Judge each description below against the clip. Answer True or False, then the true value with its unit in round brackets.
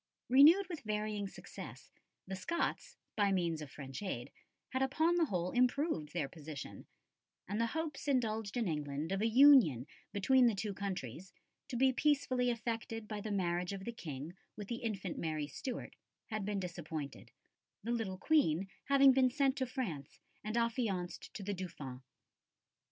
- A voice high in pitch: True (210 Hz)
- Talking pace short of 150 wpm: False (160 wpm)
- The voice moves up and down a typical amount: False (6.5 semitones)